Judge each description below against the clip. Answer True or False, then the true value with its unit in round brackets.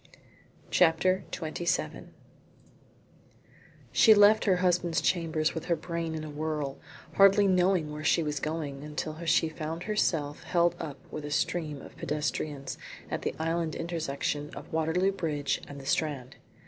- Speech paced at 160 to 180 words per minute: False (145 wpm)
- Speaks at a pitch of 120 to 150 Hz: False (160 Hz)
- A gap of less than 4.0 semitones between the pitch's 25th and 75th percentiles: True (2.8 semitones)